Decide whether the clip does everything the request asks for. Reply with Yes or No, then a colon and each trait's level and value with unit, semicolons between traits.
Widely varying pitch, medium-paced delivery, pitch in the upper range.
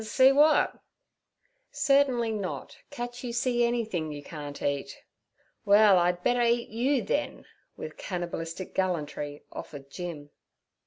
No: wide, 6.7 semitones; slow, 115 wpm; high, 205 Hz